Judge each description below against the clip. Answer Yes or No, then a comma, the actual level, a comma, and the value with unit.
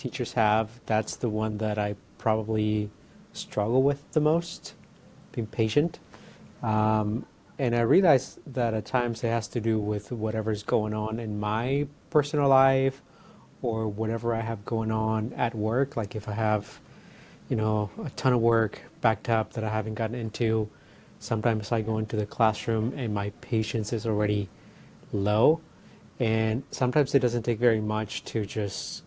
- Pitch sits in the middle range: No, low, 110 Hz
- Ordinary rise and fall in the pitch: No, narrow, 2.2 semitones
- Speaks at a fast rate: No, average, 165 wpm